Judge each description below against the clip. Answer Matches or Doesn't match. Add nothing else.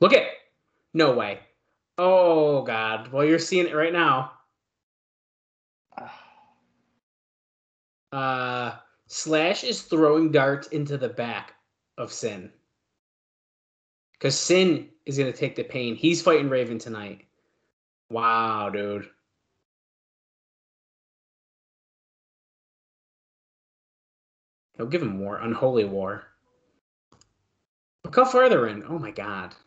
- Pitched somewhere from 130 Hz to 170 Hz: Matches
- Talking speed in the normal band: Doesn't match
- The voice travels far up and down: Matches